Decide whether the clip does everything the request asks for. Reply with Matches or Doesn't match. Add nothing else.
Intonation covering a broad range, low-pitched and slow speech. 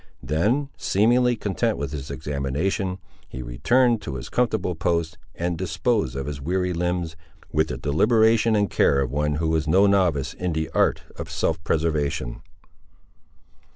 Doesn't match